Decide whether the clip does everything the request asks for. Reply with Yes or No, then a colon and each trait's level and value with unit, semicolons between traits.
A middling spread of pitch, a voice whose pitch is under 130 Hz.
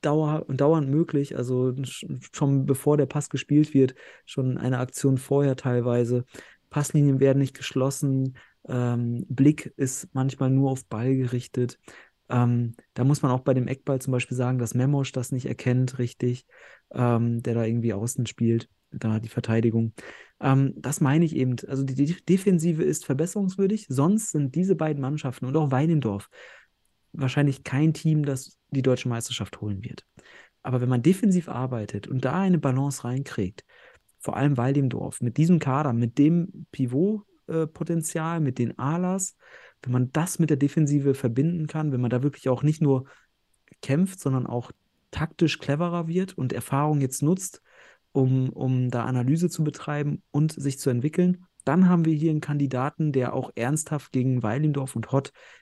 No: average, 3.4 semitones; low, 135 Hz